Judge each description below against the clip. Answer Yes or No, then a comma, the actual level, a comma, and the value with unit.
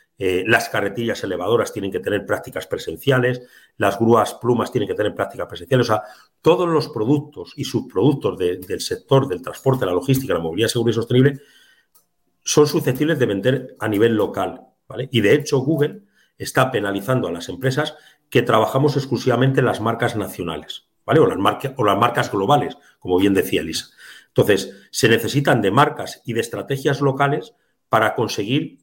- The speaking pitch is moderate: No, low, 130 Hz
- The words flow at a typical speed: Yes, average, 175 wpm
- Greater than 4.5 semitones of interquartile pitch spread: No, average, 4.1 semitones